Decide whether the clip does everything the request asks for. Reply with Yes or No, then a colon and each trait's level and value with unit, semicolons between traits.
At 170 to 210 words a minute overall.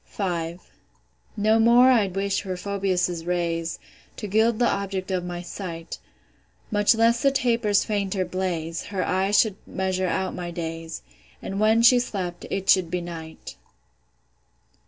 No: average, 145 wpm